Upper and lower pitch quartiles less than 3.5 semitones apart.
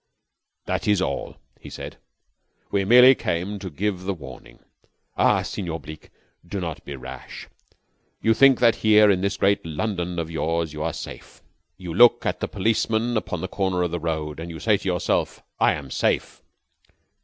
No: average, 4.2 semitones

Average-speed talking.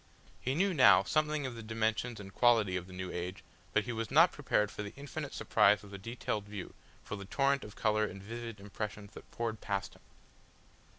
No: fast, 210 wpm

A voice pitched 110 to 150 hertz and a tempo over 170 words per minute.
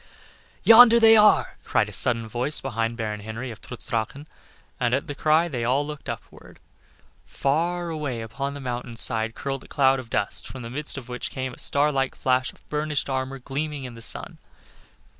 Yes: low, 135 Hz; average, 190 wpm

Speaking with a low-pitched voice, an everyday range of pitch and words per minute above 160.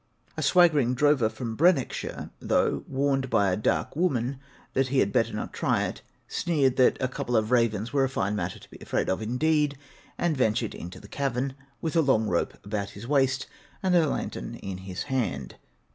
Yes: low, 130 Hz; average, 4.6 semitones; average, 190 wpm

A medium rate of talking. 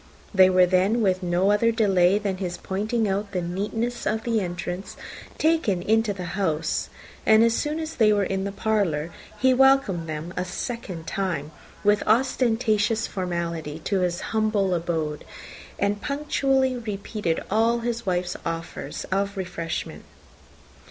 Yes: average, 145 wpm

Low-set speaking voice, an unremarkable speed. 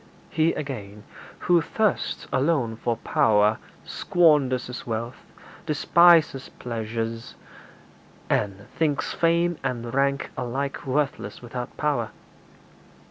No: low, 130 Hz; slow, 95 wpm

